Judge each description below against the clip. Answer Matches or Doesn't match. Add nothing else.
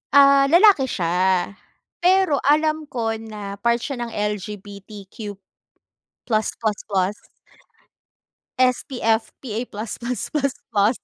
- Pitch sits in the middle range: Doesn't match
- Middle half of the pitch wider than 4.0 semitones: Matches